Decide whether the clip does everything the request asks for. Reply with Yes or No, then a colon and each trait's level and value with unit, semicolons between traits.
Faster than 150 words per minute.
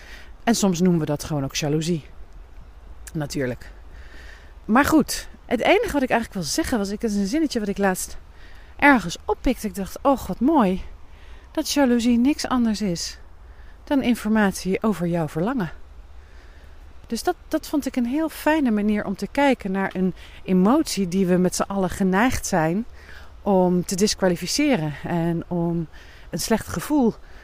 Yes: average, 160 wpm